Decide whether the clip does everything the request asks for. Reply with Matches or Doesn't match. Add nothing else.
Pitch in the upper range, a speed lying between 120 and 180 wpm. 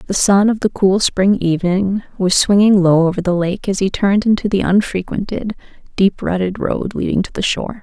Doesn't match